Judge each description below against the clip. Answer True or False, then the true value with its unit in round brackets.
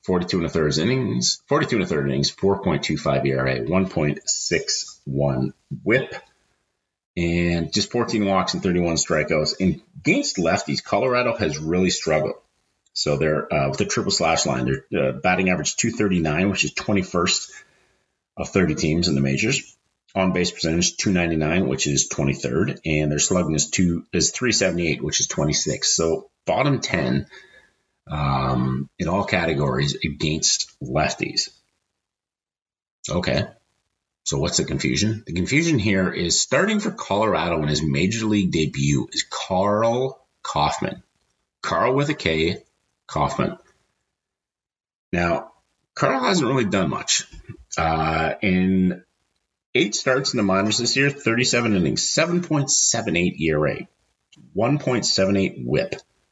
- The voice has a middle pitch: False (90 Hz)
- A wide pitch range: True (6.2 semitones)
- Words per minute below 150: True (140 wpm)